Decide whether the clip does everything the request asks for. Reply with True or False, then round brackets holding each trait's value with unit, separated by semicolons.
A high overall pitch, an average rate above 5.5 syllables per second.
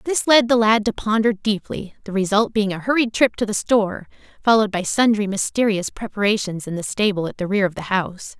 True (210 Hz; 5.8 syllables/s)